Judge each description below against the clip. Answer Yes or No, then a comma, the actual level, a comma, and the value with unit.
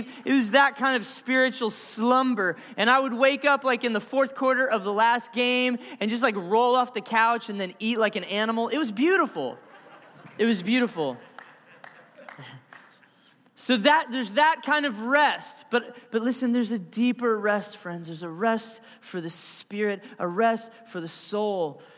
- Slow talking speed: No, average, 180 wpm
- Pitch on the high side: Yes, high, 235 Hz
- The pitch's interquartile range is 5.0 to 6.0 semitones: No, average, 3.5 semitones